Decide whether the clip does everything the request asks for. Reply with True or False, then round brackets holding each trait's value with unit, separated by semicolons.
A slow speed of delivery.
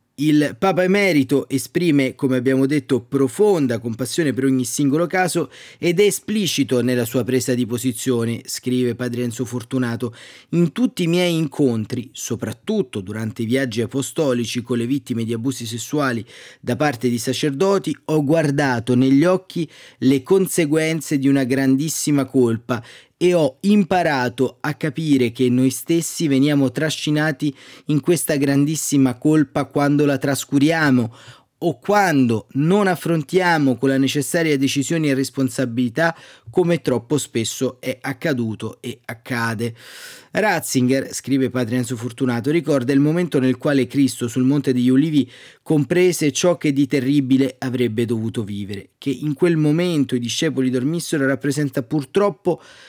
False (135 wpm)